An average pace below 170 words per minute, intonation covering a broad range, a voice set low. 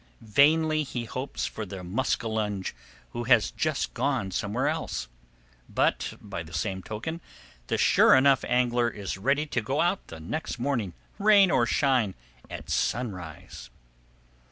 Yes: slow, 135 wpm; wide, 5.9 semitones; low, 120 Hz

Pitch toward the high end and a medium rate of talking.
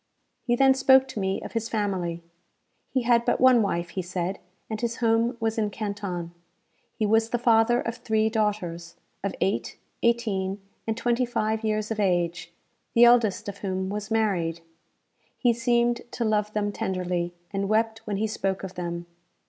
Yes: high, 215 Hz; average, 170 wpm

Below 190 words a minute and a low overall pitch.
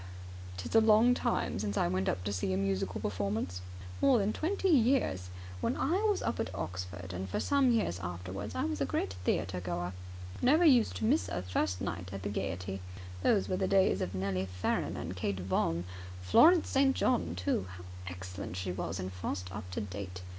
No: average, 195 wpm; very low, 95 Hz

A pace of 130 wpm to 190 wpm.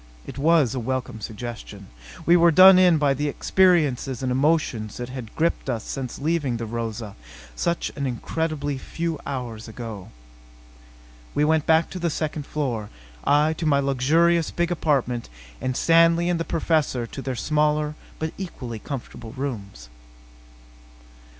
Yes: average, 150 wpm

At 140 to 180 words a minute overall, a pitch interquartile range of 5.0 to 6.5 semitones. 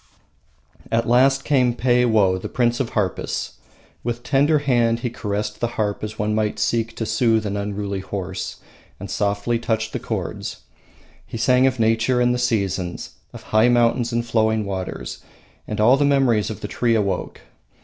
No: average, 170 wpm; narrow, 2.6 semitones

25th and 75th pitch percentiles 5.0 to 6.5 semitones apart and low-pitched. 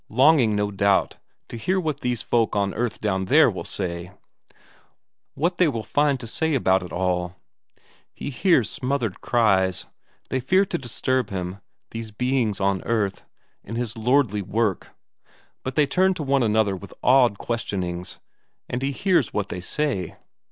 Yes: wide, 5.5 semitones; low, 115 Hz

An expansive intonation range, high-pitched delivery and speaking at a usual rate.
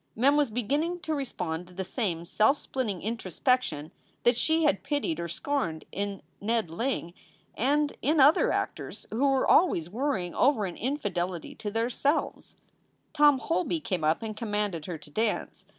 Yes: wide, 7.8 semitones; high, 225 Hz; average, 165 wpm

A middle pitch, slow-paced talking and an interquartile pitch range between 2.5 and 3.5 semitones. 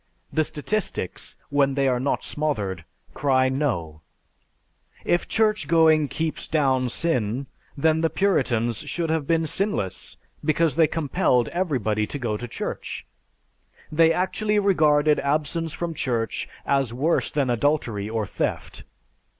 No: medium, 145 Hz; slow, 130 wpm; average, 4.8 semitones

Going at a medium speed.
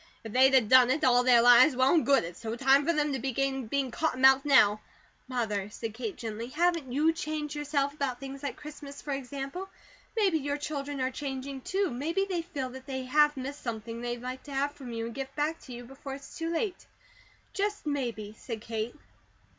No: fast, 210 wpm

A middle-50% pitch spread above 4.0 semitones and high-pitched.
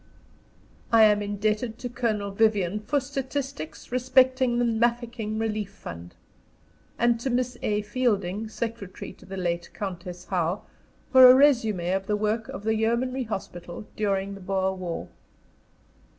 No: average, 3.7 semitones; high, 215 Hz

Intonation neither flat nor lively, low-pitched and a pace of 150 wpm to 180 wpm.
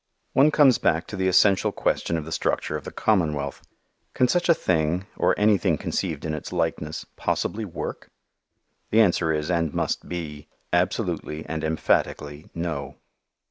Yes: average, 3.9 semitones; very low, 85 Hz; average, 155 wpm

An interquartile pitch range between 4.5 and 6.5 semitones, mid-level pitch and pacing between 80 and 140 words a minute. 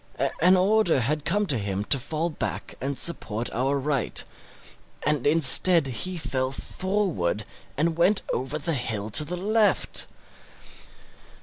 Yes: wide, 5.4 semitones; medium, 150 Hz; slow, 135 wpm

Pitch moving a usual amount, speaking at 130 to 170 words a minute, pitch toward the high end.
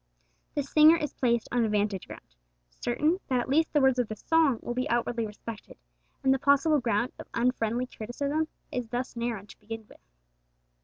No: average, 3.9 semitones; average, 185 wpm; high, 245 Hz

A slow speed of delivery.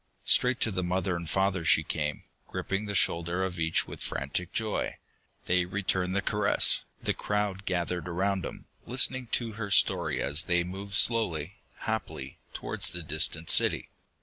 No: average, 160 wpm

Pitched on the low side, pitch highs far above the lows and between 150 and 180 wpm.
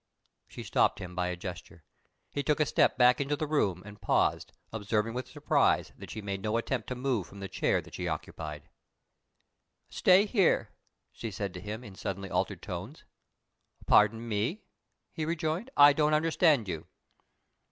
Yes: low, 110 Hz; wide, 7.0 semitones; average, 170 wpm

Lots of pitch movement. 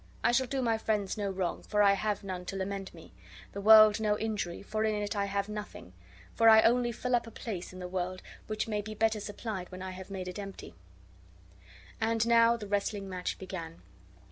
No: narrow, 2.6 semitones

